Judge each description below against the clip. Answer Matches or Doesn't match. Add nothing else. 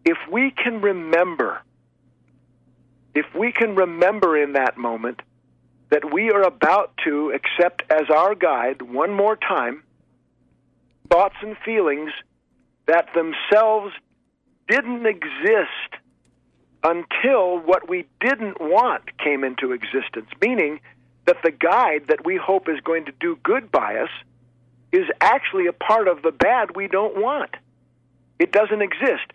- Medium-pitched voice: Matches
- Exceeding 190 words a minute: Doesn't match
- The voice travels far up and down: Matches